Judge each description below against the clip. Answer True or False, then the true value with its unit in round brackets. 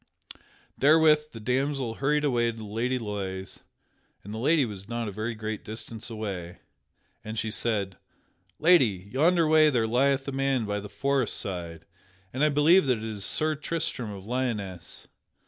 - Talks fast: False (165 wpm)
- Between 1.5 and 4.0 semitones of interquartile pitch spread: False (5.1 semitones)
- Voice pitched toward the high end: False (115 Hz)